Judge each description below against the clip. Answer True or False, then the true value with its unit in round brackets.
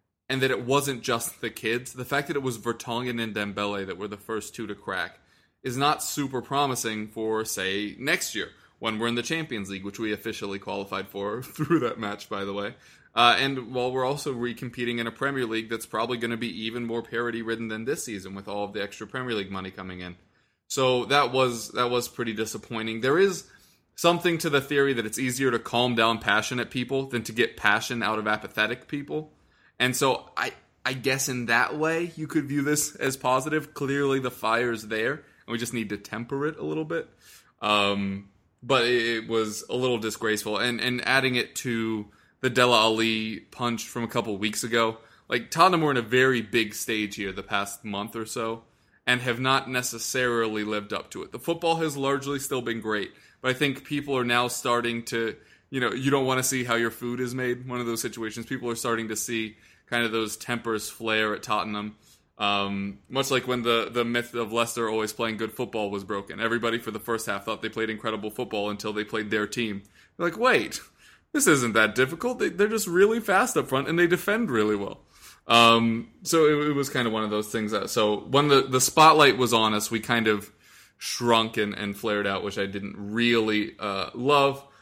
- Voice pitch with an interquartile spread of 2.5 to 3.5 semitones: True (3.2 semitones)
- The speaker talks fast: True (215 wpm)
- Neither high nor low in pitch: False (115 Hz)